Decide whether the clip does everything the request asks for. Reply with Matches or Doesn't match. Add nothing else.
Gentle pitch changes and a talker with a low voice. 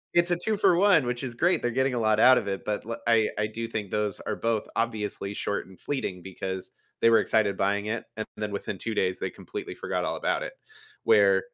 Doesn't match